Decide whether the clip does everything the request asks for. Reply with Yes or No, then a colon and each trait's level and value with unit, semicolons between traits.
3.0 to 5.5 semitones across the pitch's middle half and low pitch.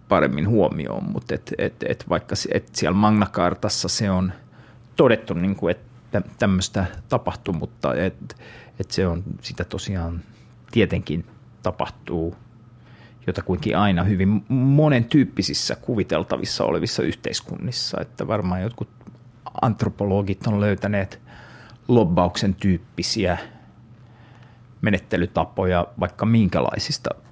Yes: average, 4.0 semitones; low, 105 Hz